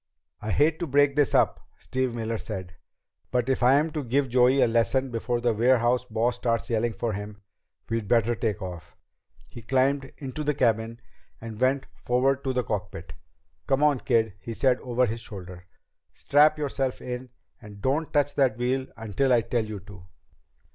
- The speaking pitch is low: Yes, low, 120 Hz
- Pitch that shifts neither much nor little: Yes, average, 3.1 semitones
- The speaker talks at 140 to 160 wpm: No, average, 175 wpm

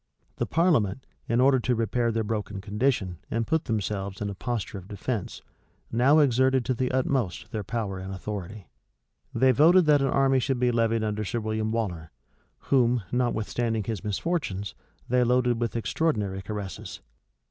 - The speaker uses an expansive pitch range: No, average, 3.7 semitones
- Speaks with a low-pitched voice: Yes, low, 115 Hz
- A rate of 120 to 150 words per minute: No, average, 160 wpm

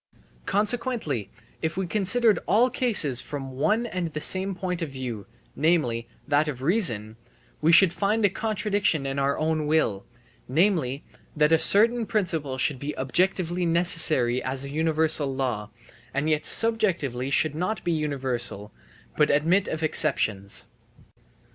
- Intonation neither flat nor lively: No, wide, 5.8 semitones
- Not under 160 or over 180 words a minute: No, average, 140 wpm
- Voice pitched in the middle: Yes, medium, 155 Hz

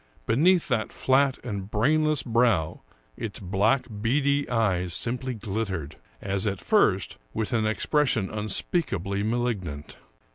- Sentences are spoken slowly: Yes, slow, 120 wpm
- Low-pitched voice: Yes, low, 110 Hz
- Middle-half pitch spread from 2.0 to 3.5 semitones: No, average, 4.9 semitones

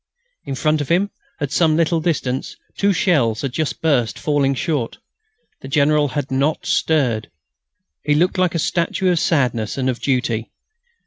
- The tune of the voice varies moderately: Yes, average, 3.9 semitones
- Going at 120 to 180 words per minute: Yes, average, 165 wpm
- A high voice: No, medium, 145 Hz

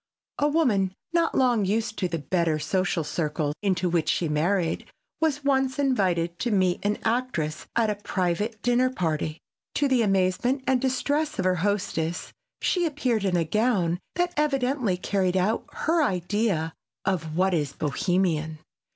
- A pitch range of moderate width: No, wide, 6.7 semitones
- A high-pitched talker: Yes, high, 195 Hz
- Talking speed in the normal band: Yes, average, 155 wpm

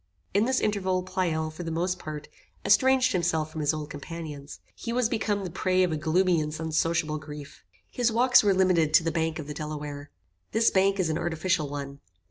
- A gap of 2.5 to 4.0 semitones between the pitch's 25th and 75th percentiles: Yes, average, 3.6 semitones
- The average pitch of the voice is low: No, medium, 165 Hz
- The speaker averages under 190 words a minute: No, average, 200 wpm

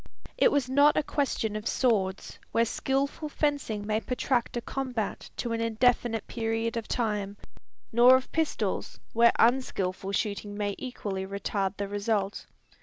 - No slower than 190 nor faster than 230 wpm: No, average, 145 wpm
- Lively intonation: No, average, 3.9 semitones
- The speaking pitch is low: No, high, 230 Hz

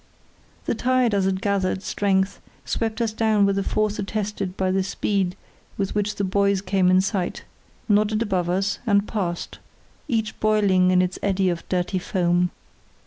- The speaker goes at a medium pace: Yes, average, 160 wpm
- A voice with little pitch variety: Yes, narrow, 2.1 semitones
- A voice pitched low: No, high, 195 Hz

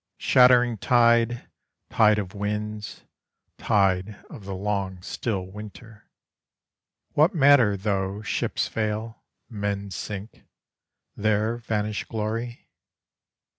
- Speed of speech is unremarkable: No, slow, 95 wpm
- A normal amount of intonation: No, narrow, 2.3 semitones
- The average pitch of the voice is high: No, low, 105 Hz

